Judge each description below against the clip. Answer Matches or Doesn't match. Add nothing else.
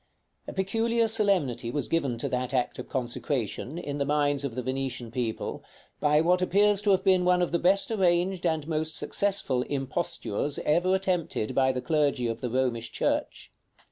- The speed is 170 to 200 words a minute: Matches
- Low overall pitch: Doesn't match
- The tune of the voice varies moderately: Doesn't match